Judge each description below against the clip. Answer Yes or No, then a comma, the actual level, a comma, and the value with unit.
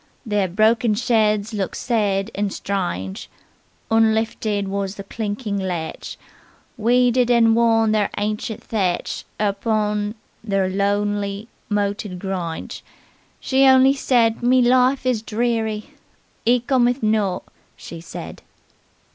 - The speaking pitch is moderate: No, high, 215 Hz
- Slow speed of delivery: Yes, slow, 115 wpm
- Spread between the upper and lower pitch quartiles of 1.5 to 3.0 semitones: Yes, average, 2.7 semitones